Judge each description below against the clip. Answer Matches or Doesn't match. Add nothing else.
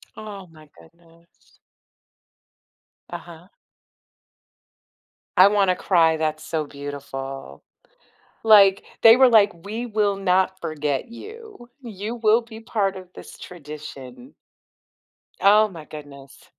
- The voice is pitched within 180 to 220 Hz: Matches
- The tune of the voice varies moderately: Doesn't match